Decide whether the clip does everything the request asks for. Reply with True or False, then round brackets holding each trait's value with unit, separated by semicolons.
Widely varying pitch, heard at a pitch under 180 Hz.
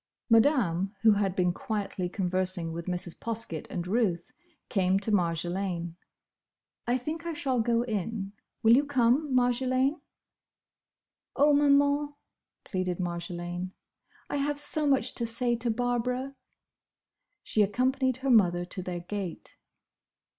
False (6.2 semitones; 220 Hz)